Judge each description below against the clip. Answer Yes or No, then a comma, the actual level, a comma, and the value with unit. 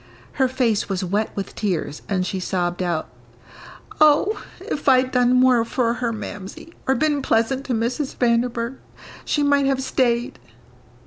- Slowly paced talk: No, average, 150 wpm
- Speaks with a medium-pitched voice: No, high, 240 Hz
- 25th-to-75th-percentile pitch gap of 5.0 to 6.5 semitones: No, average, 4.2 semitones